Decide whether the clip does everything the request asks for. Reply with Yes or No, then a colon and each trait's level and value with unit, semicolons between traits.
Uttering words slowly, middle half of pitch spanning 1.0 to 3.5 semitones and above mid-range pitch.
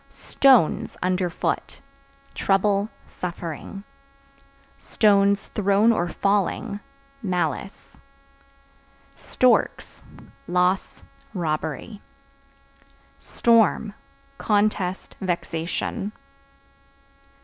Yes: slow, 50 wpm; average, 2.7 semitones; high, 195 Hz